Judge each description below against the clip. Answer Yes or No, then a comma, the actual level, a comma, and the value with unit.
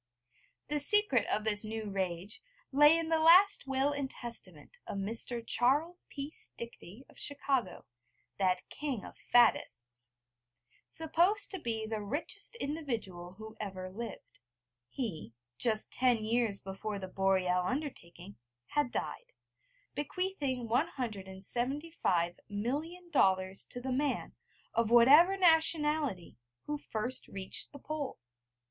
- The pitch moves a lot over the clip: Yes, wide, 7.0 semitones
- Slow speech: Yes, slow, 120 wpm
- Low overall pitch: No, high, 240 Hz